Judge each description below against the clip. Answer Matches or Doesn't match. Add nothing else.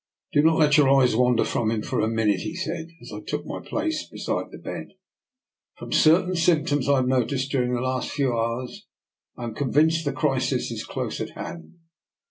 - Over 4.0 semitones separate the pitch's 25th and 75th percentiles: Matches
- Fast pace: Matches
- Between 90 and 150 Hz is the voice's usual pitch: Matches